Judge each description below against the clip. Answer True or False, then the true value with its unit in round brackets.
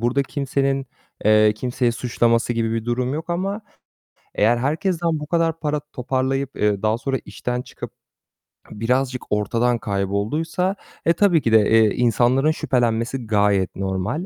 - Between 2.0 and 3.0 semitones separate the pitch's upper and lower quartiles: False (4.3 semitones)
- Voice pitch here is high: False (125 Hz)